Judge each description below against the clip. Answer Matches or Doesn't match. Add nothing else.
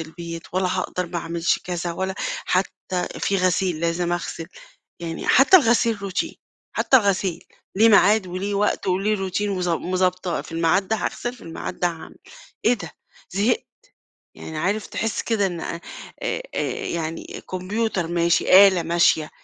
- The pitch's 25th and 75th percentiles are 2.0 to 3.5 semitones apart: Matches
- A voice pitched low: Doesn't match